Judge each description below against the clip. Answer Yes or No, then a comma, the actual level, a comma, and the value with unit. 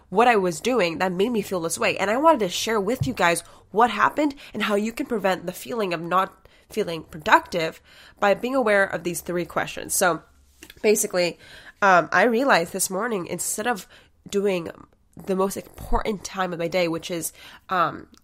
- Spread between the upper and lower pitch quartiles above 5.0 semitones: No, average, 3.8 semitones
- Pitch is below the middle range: No, high, 190 Hz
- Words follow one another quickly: No, average, 190 wpm